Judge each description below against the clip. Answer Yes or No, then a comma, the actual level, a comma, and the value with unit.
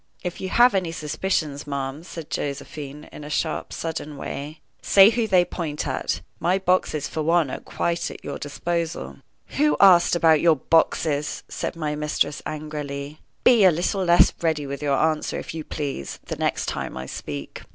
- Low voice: No, medium, 155 Hz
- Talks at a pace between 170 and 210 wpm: Yes, average, 175 wpm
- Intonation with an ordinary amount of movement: Yes, average, 3.0 semitones